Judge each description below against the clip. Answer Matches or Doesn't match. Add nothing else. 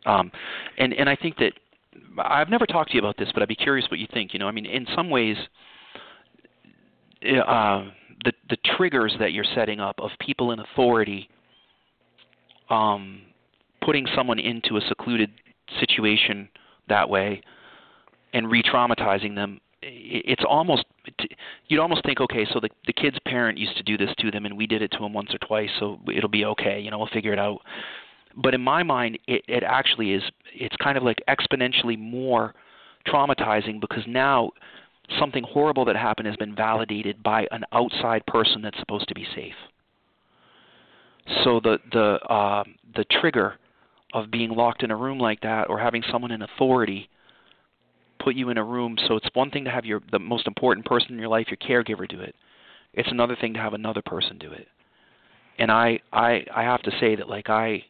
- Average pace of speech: Matches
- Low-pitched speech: Matches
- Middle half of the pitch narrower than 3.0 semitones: Matches